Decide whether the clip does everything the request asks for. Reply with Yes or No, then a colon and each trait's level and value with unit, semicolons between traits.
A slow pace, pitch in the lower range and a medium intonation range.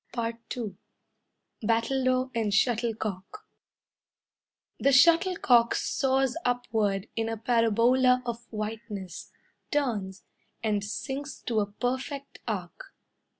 No: slow, 90 wpm; high, 235 Hz; average, 3.3 semitones